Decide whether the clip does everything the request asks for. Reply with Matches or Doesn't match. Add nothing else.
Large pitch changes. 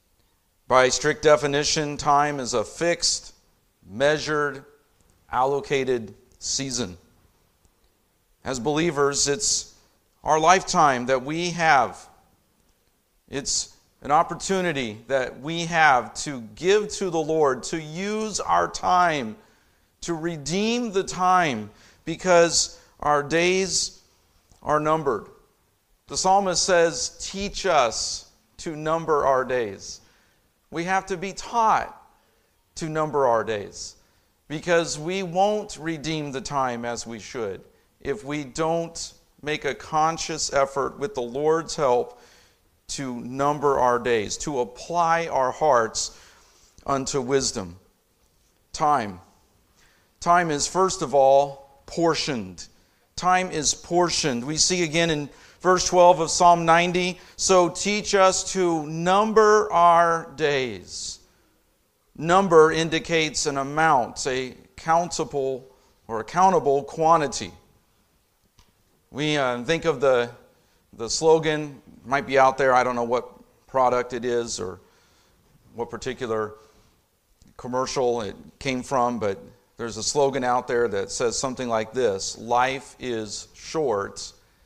Matches